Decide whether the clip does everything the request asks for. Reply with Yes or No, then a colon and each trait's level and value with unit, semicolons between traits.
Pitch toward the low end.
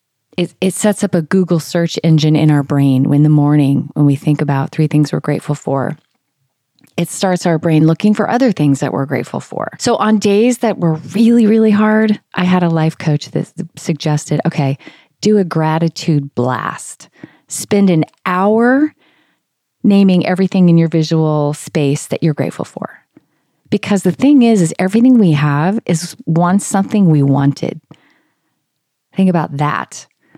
No: medium, 165 Hz